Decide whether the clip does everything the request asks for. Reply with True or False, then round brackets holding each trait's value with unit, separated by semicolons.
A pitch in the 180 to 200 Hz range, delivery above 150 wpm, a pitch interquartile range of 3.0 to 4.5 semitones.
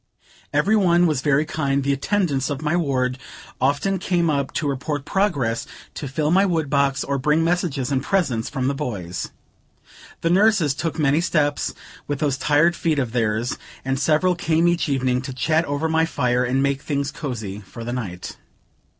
False (145 Hz; 180 wpm; 3.8 semitones)